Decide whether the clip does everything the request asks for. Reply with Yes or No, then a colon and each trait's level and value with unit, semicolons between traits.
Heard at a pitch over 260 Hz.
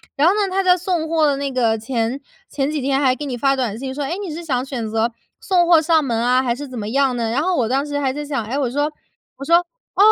Yes: very high, 275 Hz